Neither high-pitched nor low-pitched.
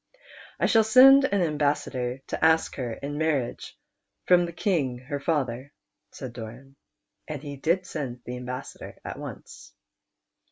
Yes: medium, 145 Hz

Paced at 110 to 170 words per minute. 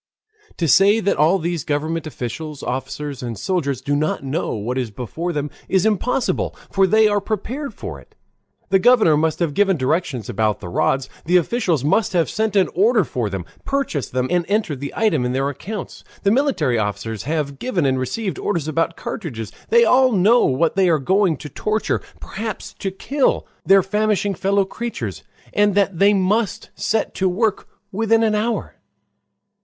No: average, 180 wpm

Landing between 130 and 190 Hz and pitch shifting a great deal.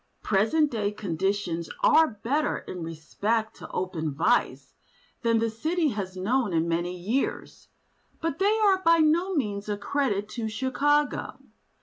No: high, 220 Hz; wide, 7.3 semitones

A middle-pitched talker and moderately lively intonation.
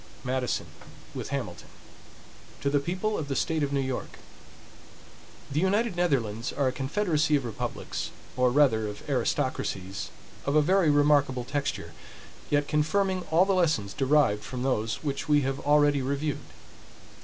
Yes: medium, 145 Hz; average, 3.2 semitones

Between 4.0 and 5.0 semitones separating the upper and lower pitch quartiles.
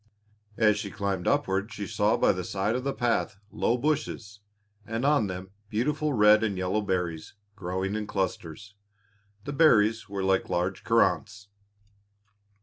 No: average, 3.0 semitones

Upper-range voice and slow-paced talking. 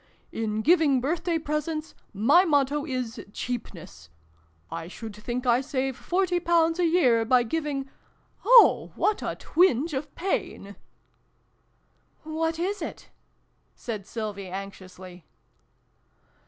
Yes: very high, 270 Hz; slow, 125 wpm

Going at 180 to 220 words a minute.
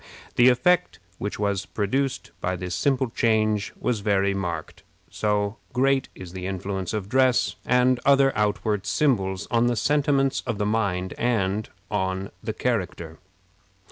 No: average, 140 wpm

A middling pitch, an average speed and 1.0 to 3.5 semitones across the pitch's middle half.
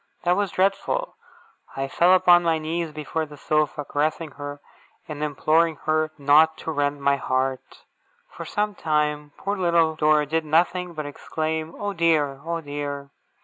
Yes: medium, 155 Hz; average, 160 wpm; narrow, 2.4 semitones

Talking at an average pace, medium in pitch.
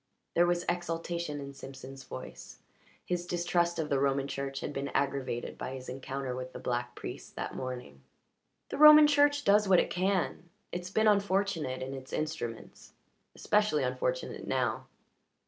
Yes: average, 155 wpm; medium, 145 Hz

